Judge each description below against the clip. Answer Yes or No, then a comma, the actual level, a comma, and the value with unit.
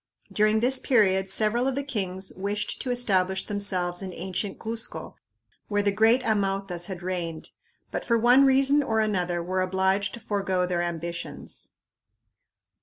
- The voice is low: No, high, 200 Hz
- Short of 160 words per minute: Yes, average, 150 wpm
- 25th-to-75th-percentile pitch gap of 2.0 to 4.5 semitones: Yes, average, 3.3 semitones